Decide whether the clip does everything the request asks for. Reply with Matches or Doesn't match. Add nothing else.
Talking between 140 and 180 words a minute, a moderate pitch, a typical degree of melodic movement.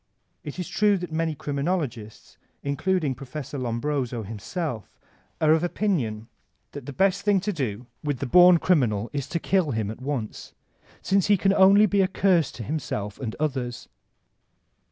Doesn't match